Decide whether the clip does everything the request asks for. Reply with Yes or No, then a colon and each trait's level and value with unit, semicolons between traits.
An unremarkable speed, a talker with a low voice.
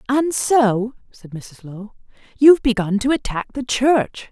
No: average, 155 wpm; high, 235 Hz